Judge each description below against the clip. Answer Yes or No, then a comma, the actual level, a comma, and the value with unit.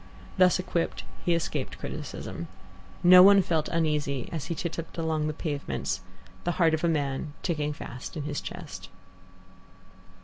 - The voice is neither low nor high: Yes, medium, 160 Hz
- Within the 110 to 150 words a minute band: Yes, average, 145 wpm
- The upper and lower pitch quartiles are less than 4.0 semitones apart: Yes, narrow, 2.6 semitones